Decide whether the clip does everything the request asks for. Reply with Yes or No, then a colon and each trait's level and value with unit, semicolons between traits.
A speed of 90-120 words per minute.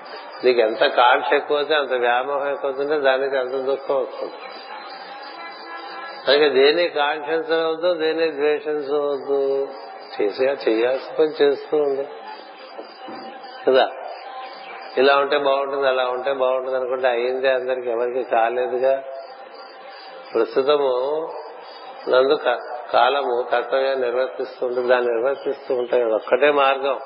Yes: average, 100 wpm